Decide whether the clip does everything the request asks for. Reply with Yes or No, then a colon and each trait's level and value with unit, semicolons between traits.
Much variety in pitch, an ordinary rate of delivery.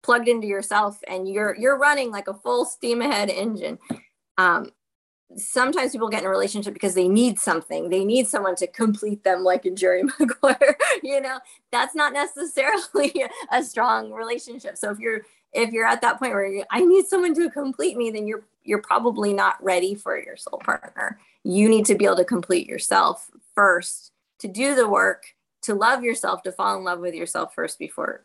Yes: wide, 5.7 semitones; average, 195 wpm